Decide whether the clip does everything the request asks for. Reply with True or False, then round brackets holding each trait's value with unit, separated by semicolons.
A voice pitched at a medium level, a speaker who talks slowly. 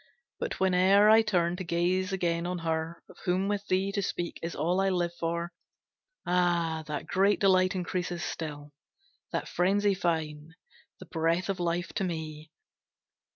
False (175 Hz; 155 wpm)